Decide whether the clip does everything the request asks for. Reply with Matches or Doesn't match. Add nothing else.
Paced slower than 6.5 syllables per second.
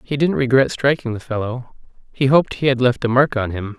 Matches